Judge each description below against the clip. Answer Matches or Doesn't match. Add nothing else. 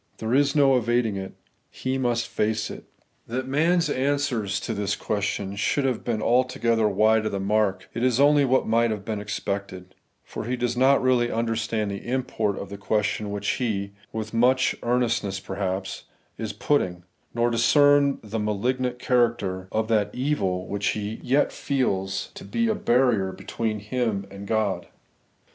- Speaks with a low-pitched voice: Matches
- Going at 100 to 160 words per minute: Doesn't match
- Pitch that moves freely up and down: Doesn't match